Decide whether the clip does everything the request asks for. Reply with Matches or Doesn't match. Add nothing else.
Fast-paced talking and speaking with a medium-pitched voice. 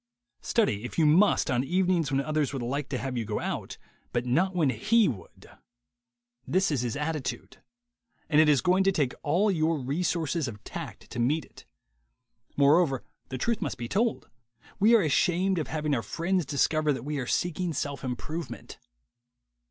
Doesn't match